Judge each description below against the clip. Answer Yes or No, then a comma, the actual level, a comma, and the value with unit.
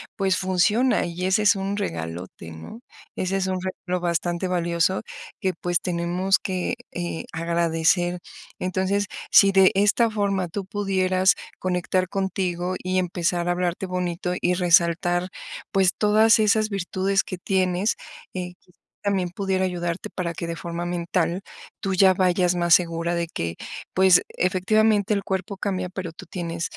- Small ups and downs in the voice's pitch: Yes, narrow, 1.9 semitones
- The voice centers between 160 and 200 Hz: Yes, medium, 185 Hz